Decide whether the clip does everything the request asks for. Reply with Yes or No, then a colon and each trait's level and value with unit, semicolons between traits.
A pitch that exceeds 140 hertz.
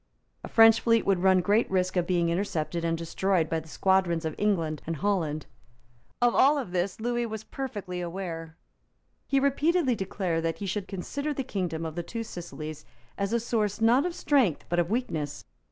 Yes: high, 190 Hz